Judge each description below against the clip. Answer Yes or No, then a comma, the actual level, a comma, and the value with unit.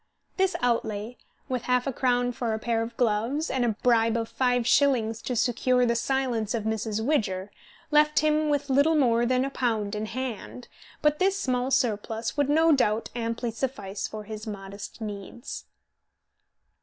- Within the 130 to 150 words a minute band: No, average, 170 wpm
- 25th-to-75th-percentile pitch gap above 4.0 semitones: No, average, 3.3 semitones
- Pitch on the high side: Yes, high, 240 Hz